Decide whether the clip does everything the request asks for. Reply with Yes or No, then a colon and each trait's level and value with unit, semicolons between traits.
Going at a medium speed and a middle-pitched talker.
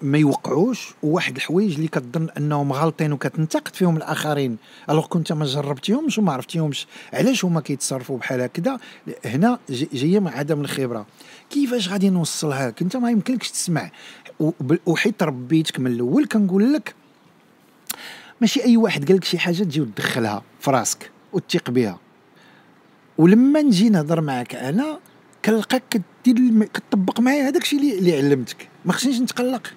No: fast, 140 wpm; medium, 175 Hz